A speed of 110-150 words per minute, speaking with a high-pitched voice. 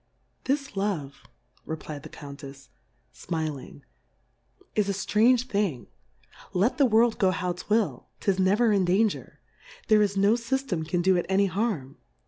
Yes: average, 145 wpm; high, 195 Hz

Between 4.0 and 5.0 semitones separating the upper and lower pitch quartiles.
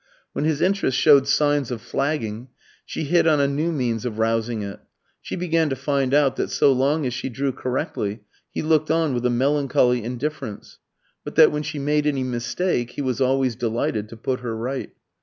No: average, 3.6 semitones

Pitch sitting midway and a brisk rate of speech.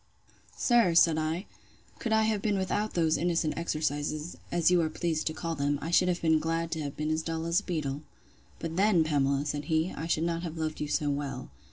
Yes: medium, 160 Hz; fast, 225 wpm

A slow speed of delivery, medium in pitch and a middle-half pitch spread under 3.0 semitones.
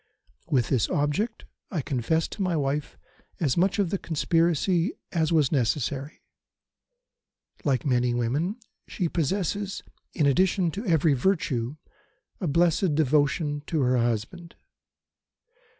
No: slow, 120 wpm; medium, 155 Hz; average, 4.4 semitones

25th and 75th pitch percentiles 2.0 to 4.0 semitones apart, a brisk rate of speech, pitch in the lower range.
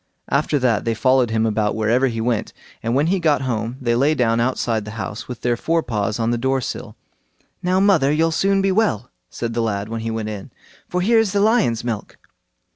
No: wide, 5.6 semitones; fast, 220 wpm; low, 120 Hz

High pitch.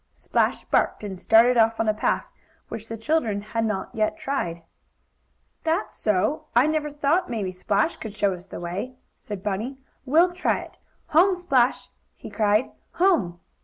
Yes: high, 225 Hz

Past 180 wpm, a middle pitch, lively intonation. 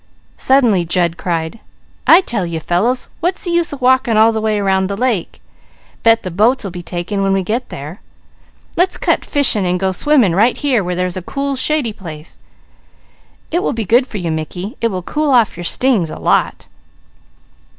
No: average, 190 wpm; high, 210 Hz; wide, 6.2 semitones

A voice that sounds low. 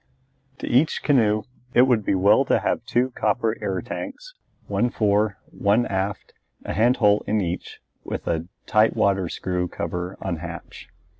Yes: low, 105 Hz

